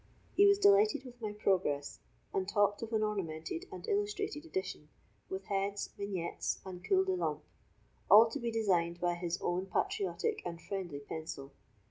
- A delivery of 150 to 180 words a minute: Yes, average, 160 wpm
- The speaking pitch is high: Yes, high, 200 Hz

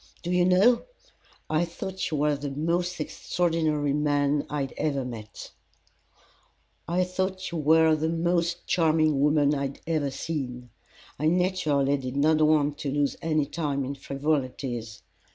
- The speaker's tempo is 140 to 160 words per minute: Yes, average, 150 wpm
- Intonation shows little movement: No, average, 3.0 semitones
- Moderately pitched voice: Yes, medium, 150 Hz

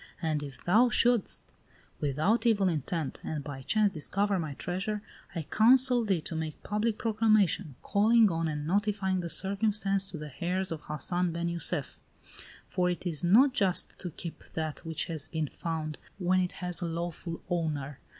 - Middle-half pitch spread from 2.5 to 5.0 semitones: Yes, average, 4.3 semitones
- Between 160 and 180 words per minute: Yes, average, 170 wpm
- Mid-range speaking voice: Yes, medium, 180 Hz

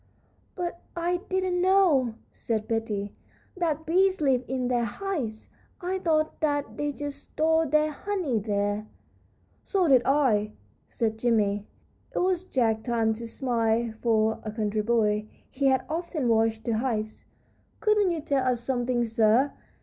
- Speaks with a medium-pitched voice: No, very high, 255 Hz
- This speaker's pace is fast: No, average, 145 wpm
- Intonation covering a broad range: Yes, wide, 6.3 semitones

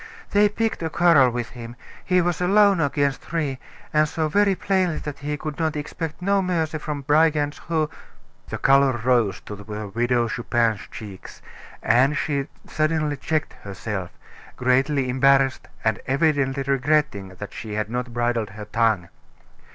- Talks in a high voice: No, medium, 140 Hz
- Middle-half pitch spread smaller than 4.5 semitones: No, average, 4.8 semitones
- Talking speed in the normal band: Yes, average, 150 wpm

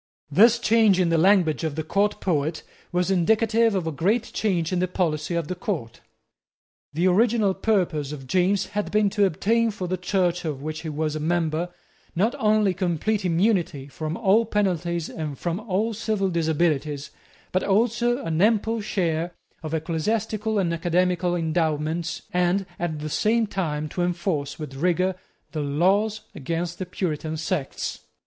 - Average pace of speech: Yes, average, 160 wpm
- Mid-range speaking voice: Yes, medium, 180 Hz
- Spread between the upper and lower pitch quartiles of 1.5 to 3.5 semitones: No, average, 4.3 semitones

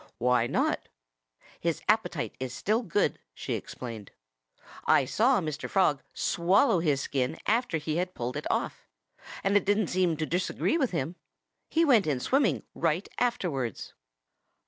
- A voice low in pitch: No, medium, 170 Hz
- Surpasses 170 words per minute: No, average, 145 wpm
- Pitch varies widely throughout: Yes, wide, 7.1 semitones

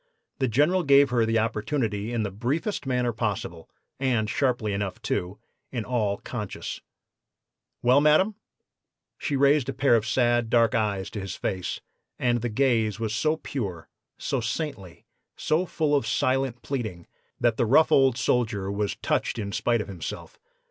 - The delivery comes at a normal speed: Yes, average, 160 wpm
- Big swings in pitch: No, average, 4.2 semitones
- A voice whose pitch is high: No, low, 120 Hz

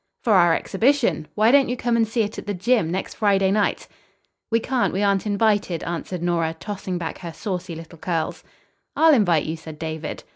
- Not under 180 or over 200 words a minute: Yes, average, 195 wpm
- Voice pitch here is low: No, high, 195 Hz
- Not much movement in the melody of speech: No, average, 4.8 semitones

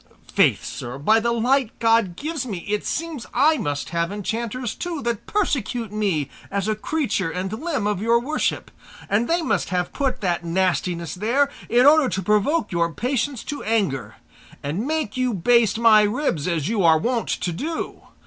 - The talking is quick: No, average, 175 wpm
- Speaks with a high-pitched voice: Yes, high, 220 Hz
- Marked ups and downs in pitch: Yes, wide, 6.0 semitones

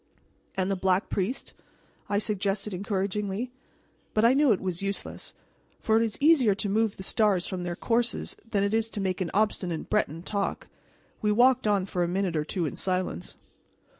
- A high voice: Yes, high, 200 Hz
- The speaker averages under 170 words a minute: No, average, 175 wpm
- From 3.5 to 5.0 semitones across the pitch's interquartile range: No, average, 2.7 semitones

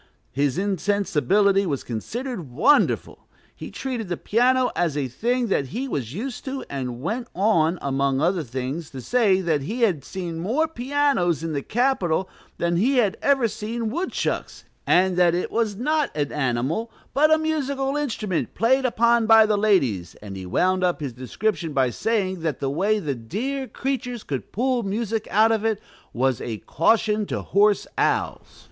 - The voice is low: No, high, 200 Hz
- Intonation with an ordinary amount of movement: No, wide, 7.9 semitones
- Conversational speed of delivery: Yes, average, 170 wpm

